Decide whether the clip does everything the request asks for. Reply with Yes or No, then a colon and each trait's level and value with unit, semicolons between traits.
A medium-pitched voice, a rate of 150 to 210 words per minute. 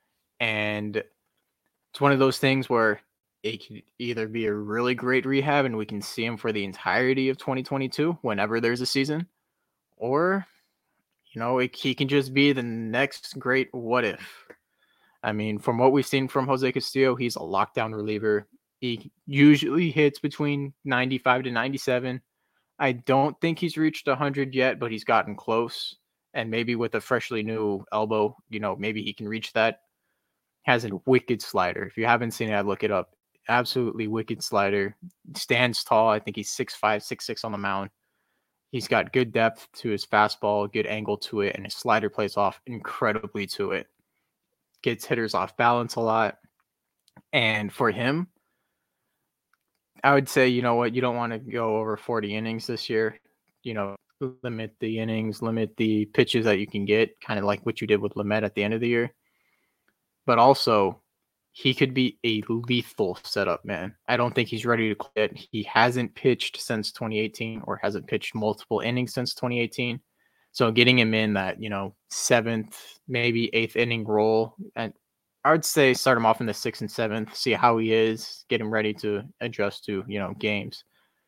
No: low, 115 Hz; average, 185 wpm